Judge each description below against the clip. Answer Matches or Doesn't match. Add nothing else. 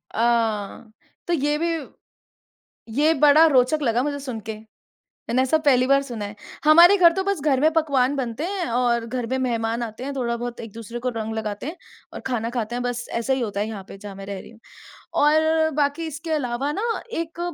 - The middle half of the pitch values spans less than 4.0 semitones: Doesn't match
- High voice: Matches